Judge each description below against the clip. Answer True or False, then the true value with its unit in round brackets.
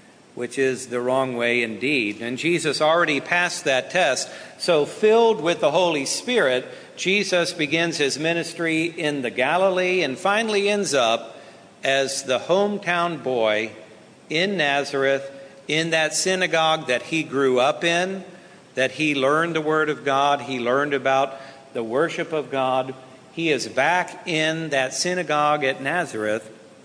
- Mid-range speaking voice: True (150 Hz)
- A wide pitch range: False (4.7 semitones)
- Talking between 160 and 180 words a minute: False (145 wpm)